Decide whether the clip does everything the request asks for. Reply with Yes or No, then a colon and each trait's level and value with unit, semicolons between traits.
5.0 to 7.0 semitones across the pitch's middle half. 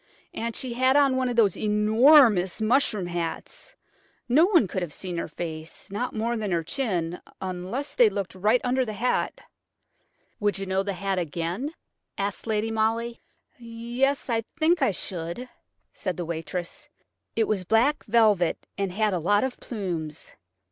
Yes: average, 5.3 semitones